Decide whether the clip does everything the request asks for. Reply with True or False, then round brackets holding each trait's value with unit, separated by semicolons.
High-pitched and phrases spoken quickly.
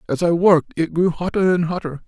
False (170 Hz; 230 wpm)